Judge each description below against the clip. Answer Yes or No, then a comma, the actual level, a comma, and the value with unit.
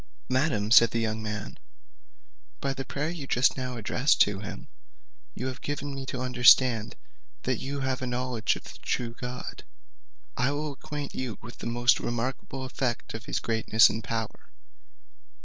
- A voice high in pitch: No, low, 125 Hz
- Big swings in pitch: No, average, 2.7 semitones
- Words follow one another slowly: No, average, 165 wpm